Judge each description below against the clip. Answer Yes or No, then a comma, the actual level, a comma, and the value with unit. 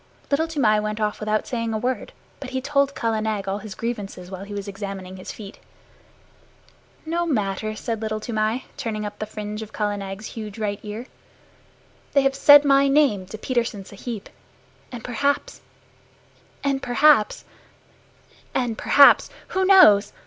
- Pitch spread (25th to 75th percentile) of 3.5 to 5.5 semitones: Yes, average, 4.2 semitones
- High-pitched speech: Yes, high, 220 Hz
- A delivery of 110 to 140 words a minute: No, average, 155 wpm